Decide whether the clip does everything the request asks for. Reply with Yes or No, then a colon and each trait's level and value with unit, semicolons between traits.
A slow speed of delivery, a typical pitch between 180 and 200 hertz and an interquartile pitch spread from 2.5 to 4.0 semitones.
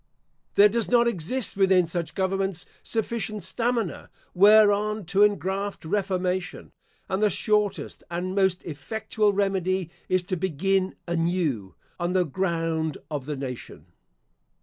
Yes: slow, 125 wpm; high, 190 Hz; average, 3.1 semitones